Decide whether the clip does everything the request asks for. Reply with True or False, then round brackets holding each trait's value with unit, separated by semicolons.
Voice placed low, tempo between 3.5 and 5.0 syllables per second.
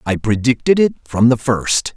True (120 Hz; 4.6 syllables/s)